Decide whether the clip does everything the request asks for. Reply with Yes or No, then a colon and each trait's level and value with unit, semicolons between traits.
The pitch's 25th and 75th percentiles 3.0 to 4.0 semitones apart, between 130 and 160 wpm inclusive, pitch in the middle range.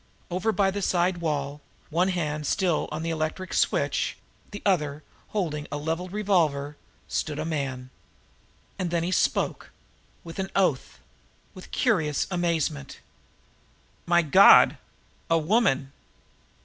Yes: average, 3.7 semitones; slow, 135 wpm; medium, 165 Hz